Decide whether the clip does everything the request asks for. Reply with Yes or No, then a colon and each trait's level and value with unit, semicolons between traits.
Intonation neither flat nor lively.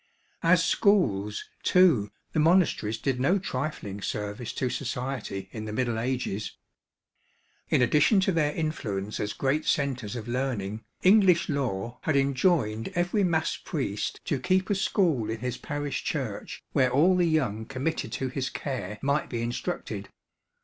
No: wide, 6.6 semitones